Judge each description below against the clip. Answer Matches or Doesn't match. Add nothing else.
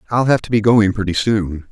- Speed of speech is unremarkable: Doesn't match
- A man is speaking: Matches